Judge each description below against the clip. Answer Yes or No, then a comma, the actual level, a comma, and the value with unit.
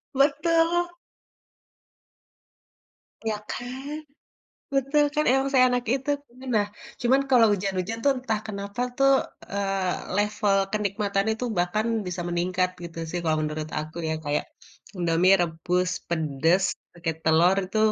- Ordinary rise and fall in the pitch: No, wide, 6.4 semitones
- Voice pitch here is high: Yes, high, 200 Hz